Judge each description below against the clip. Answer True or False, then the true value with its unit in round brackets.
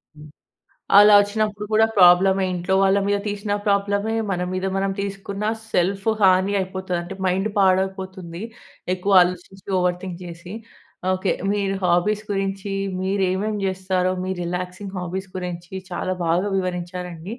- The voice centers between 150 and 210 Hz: True (190 Hz)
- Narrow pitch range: True (1.8 semitones)